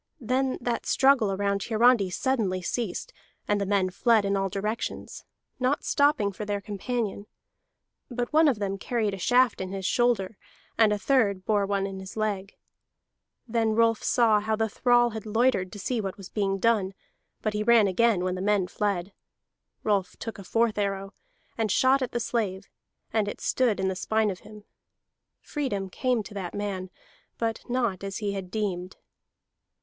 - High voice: Yes, high, 210 Hz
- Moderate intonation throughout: Yes, average, 3.1 semitones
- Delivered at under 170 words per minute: No, average, 180 wpm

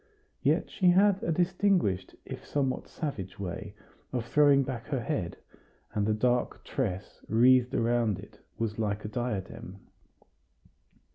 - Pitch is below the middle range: Yes, low, 120 Hz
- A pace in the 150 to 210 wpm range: No, slow, 135 wpm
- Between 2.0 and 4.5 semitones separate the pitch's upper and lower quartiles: No, average, 5.2 semitones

